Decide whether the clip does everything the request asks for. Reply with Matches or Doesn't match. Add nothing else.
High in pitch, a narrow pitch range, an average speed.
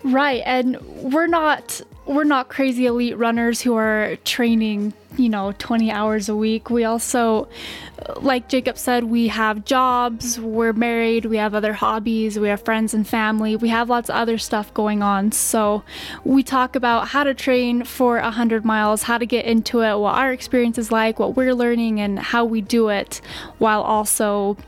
Matches